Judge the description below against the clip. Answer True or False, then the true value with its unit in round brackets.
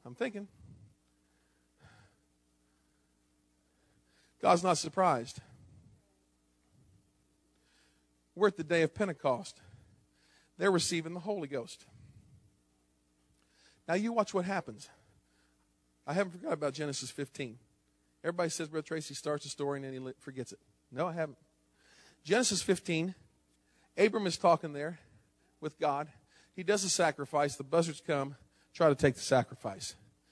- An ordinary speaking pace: False (125 wpm)